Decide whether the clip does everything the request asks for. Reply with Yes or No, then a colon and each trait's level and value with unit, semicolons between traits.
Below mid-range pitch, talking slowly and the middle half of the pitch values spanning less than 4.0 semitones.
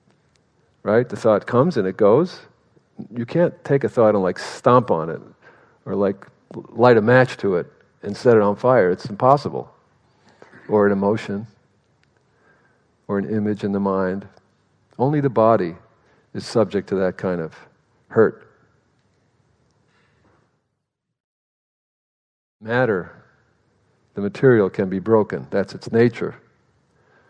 Yes: low, 105 Hz; slow, 130 wpm; average, 3.3 semitones